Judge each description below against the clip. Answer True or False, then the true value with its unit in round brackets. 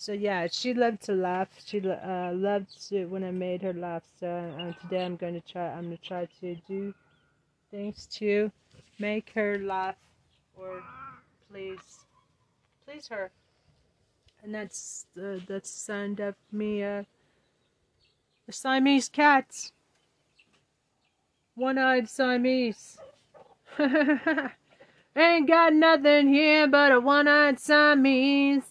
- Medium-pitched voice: False (205 Hz)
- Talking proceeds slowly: True (120 wpm)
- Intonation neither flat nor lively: False (6.5 semitones)